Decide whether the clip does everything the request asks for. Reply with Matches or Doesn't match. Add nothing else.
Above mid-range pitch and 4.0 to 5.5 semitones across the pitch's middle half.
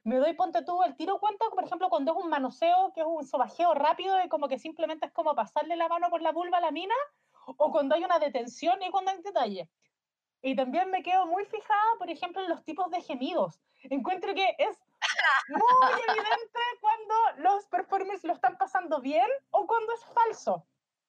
Doesn't match